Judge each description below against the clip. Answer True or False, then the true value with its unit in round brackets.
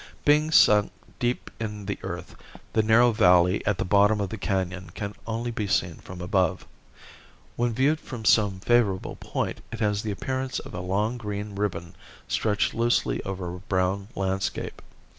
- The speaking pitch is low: True (105 Hz)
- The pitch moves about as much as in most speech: True (3.3 semitones)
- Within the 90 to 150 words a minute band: False (165 wpm)